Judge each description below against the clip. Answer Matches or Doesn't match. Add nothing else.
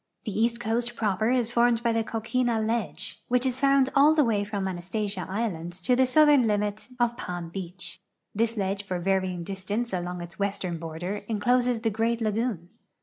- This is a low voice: Doesn't match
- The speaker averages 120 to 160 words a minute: Doesn't match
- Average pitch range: Matches